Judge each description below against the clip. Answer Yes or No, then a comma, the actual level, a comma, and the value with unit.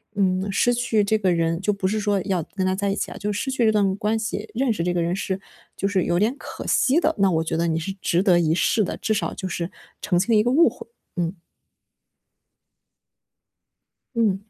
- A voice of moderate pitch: No, high, 200 Hz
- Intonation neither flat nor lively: Yes, average, 3.4 semitones